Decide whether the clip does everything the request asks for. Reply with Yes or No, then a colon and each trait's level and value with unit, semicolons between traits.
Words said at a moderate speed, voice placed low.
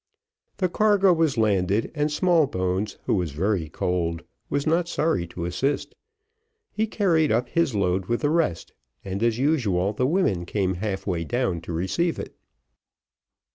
Yes: average, 155 wpm; low, 110 Hz